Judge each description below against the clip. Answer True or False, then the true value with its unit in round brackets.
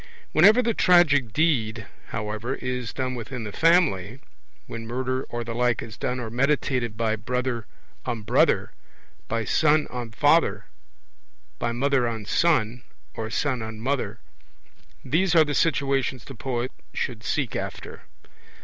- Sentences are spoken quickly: False (140 wpm)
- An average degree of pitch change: True (3.9 semitones)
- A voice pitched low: True (125 Hz)